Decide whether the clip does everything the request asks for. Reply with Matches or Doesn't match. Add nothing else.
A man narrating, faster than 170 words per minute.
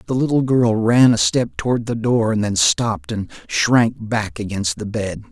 Matches